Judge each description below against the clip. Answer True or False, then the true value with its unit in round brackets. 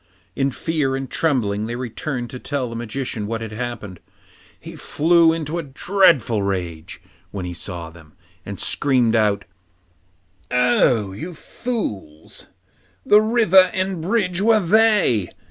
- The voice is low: True (125 Hz)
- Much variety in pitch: True (8.6 semitones)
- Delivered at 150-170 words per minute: False (135 wpm)